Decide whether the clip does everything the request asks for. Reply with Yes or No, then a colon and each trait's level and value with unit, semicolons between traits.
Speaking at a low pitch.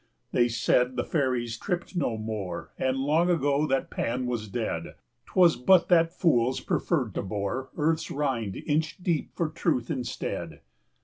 Yes: low, 130 Hz